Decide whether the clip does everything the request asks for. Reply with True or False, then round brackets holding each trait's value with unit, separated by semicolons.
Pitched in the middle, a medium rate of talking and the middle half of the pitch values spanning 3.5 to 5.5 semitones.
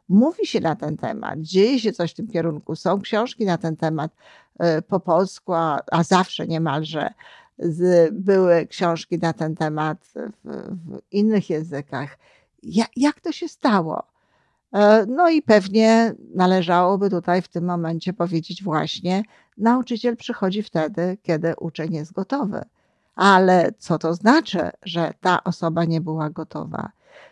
True (180 Hz; 130 wpm; 4.4 semitones)